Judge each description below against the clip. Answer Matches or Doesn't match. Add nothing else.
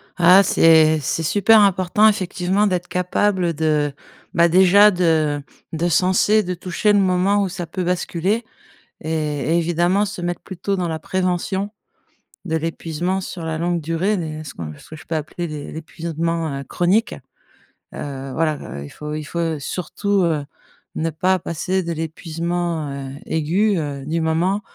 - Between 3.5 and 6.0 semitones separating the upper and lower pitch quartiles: Doesn't match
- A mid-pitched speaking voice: Matches